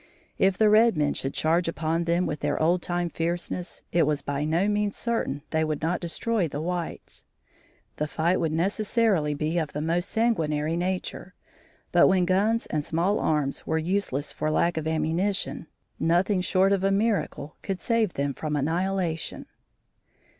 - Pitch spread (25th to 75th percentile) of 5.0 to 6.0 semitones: No, average, 3.8 semitones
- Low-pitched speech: No, medium, 170 Hz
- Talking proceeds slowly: No, average, 170 wpm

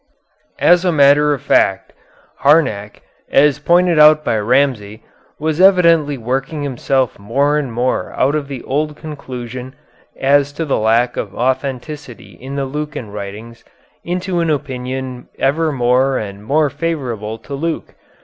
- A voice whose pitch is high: No, low, 135 Hz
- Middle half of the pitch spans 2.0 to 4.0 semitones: Yes, average, 3.7 semitones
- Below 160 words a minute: Yes, average, 140 wpm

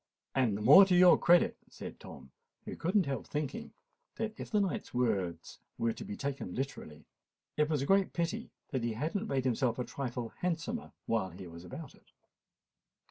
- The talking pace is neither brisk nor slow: Yes, average, 190 wpm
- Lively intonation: Yes, wide, 7.6 semitones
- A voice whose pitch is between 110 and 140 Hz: Yes, low, 135 Hz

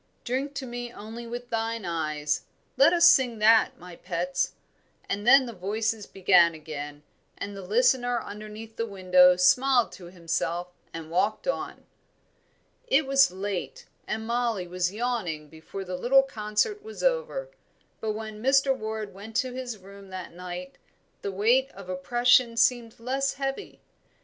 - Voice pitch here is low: No, high, 215 Hz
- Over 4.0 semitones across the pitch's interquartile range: Yes, average, 5.2 semitones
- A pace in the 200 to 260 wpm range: No, average, 150 wpm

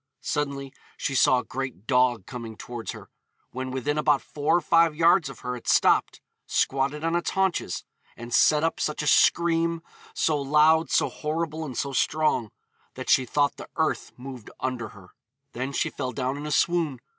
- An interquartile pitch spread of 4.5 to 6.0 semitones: No, average, 3.5 semitones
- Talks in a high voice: No, medium, 140 Hz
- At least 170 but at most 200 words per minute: Yes, average, 180 wpm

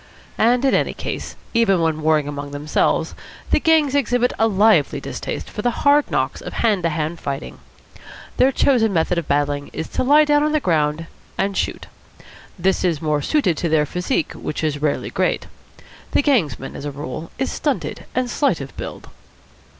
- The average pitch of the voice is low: No, medium, 180 Hz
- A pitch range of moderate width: No, wide, 8.7 semitones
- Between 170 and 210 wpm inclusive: Yes, average, 180 wpm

